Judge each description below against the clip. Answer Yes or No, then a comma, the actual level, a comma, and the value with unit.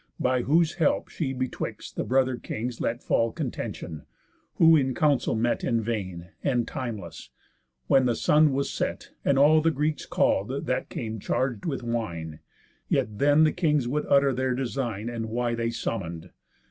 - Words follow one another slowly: No, average, 165 wpm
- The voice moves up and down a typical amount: Yes, average, 3.7 semitones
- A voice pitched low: Yes, low, 125 Hz